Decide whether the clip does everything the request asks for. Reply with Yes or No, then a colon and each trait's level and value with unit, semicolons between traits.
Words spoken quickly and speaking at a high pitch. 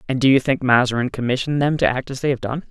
No: fast, 290 wpm; low, 130 Hz